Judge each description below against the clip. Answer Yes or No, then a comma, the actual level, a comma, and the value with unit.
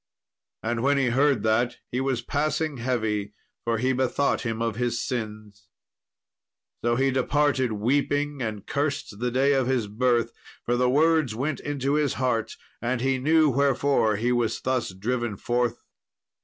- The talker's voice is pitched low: Yes, low, 125 Hz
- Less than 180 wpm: Yes, average, 155 wpm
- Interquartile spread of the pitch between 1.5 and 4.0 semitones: Yes, average, 3.2 semitones